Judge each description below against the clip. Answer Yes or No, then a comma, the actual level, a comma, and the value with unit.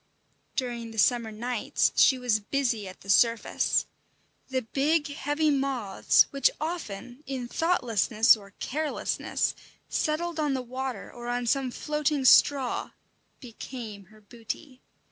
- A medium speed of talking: No, slow, 125 wpm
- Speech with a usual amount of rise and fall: Yes, average, 3.9 semitones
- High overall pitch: Yes, very high, 250 Hz